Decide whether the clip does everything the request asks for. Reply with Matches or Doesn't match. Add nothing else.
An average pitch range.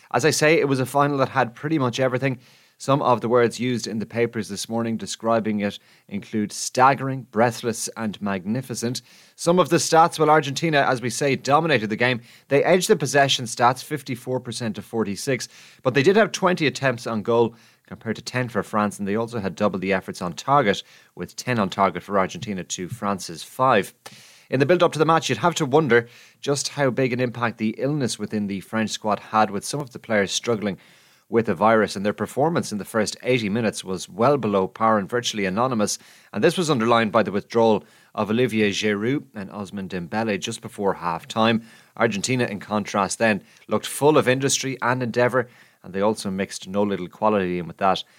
Matches